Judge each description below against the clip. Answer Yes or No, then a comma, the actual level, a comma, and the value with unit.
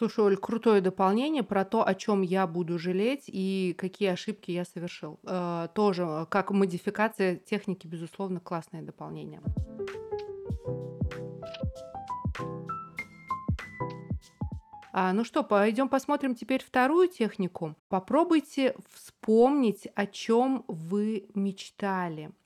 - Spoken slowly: Yes, slow, 100 wpm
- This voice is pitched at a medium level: No, high, 195 Hz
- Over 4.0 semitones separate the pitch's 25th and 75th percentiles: Yes, average, 4.7 semitones